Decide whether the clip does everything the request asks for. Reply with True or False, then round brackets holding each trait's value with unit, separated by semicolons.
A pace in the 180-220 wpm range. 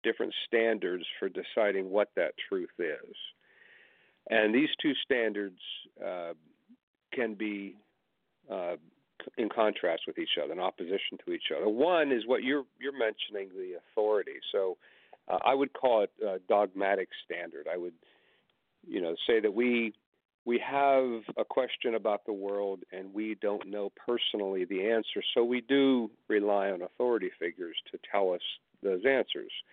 False (155 wpm)